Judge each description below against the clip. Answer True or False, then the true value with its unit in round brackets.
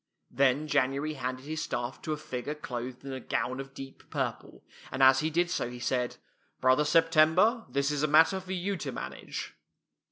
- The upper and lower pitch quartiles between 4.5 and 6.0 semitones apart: False (3.4 semitones)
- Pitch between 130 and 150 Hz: True (140 Hz)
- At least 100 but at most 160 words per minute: False (200 wpm)